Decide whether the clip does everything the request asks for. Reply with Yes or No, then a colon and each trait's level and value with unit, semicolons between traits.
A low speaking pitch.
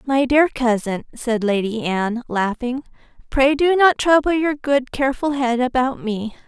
No: very high, 255 Hz